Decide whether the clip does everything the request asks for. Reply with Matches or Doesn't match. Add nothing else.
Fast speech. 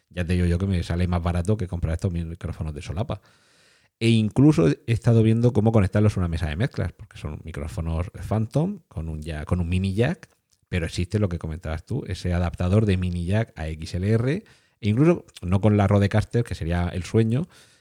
Matches